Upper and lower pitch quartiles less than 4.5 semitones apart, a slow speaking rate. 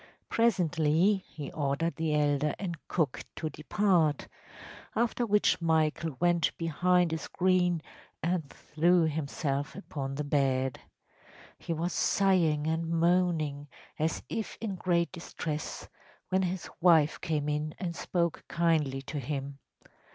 Yes: average, 3.1 semitones; slow, 125 wpm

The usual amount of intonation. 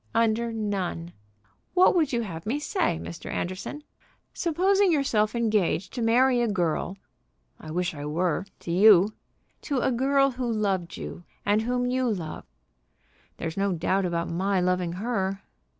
No: wide, 5.7 semitones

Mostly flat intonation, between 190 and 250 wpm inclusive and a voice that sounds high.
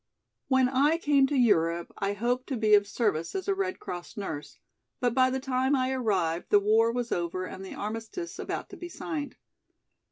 No: average, 4.9 semitones; average, 195 wpm; high, 240 Hz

